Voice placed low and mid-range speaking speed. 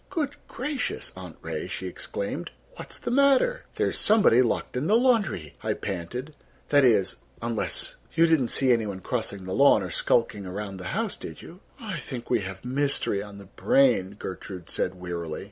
Yes: low, 120 Hz; average, 175 wpm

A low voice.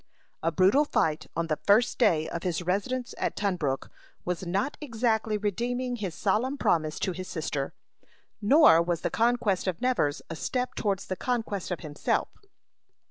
No: high, 195 Hz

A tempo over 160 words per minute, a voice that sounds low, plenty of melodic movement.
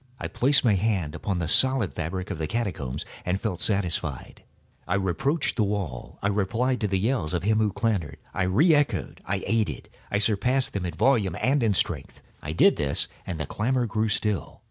No: average, 190 wpm; low, 100 Hz; average, 4.5 semitones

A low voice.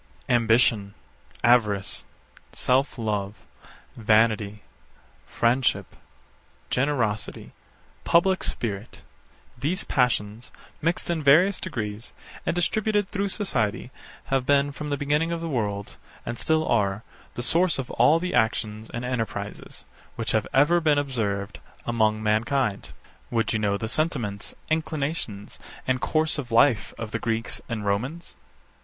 Yes: low, 120 Hz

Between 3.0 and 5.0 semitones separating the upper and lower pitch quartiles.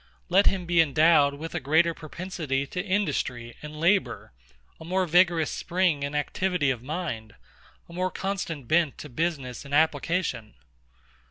Yes: average, 4.0 semitones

